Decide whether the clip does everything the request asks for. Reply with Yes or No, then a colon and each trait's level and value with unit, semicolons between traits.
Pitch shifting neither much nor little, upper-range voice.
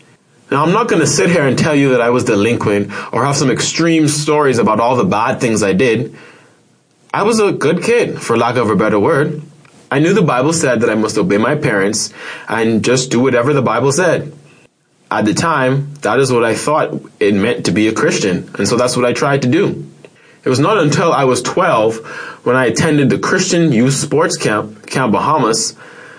No: average, 4.8 semitones; medium, 140 Hz